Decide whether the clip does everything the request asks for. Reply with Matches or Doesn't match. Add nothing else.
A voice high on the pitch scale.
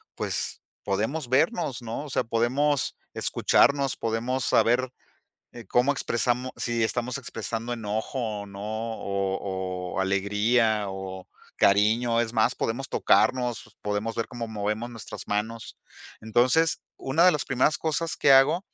Doesn't match